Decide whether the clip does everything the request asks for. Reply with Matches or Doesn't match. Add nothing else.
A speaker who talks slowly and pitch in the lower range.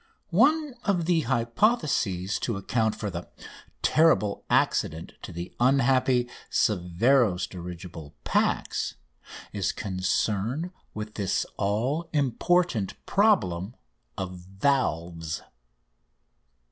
Matches